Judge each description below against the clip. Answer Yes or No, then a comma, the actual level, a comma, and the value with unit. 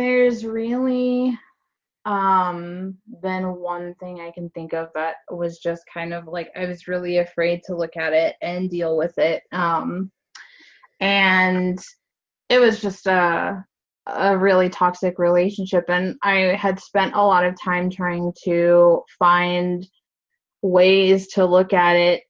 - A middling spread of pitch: No, narrow, 1.9 semitones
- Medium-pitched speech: Yes, medium, 180 Hz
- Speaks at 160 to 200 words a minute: No, average, 145 wpm